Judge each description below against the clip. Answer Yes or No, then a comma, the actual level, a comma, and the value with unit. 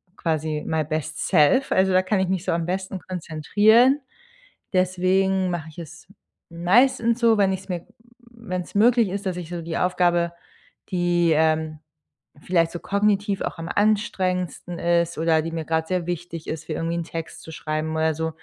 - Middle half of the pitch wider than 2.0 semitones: Yes, average, 2.8 semitones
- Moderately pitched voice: Yes, medium, 175 Hz